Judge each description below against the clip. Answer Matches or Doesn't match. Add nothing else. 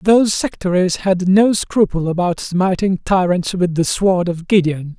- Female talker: Doesn't match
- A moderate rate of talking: Matches